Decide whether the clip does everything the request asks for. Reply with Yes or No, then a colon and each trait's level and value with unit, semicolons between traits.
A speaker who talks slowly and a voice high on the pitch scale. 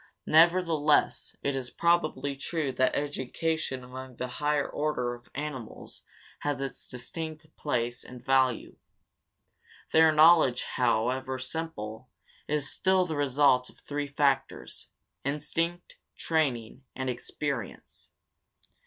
No: slow, 110 wpm; medium, 140 Hz